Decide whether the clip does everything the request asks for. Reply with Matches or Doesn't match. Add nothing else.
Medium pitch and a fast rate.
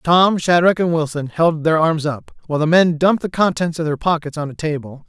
Matches